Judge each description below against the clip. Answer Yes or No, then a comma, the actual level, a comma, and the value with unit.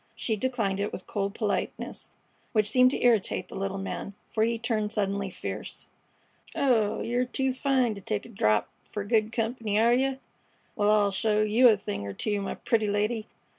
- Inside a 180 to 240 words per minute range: Yes, average, 185 wpm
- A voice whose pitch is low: No, high, 215 Hz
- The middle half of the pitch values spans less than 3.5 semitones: Yes, average, 2.8 semitones